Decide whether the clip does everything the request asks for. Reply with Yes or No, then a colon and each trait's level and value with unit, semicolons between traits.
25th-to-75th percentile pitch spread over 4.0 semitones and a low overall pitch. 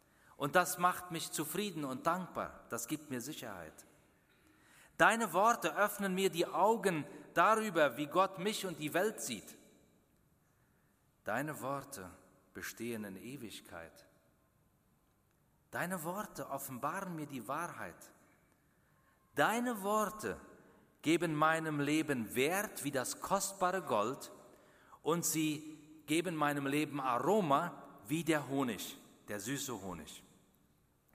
No: average, 4.7 semitones; medium, 155 Hz